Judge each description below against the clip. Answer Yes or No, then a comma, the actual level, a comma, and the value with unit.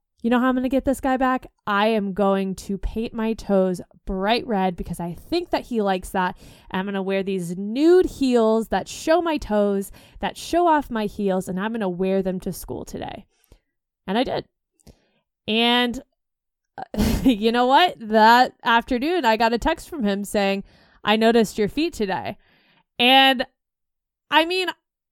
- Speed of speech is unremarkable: Yes, average, 185 wpm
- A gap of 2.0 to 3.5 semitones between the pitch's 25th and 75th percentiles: No, average, 5.0 semitones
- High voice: Yes, high, 225 Hz